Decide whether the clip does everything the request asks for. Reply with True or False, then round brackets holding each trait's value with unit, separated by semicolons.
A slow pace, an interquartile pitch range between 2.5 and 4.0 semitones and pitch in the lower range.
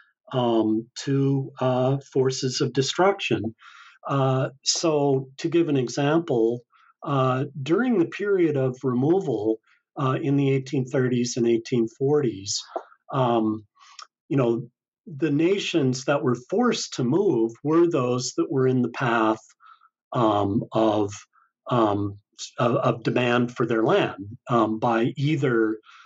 True (120 wpm; 3.6 semitones; 130 Hz)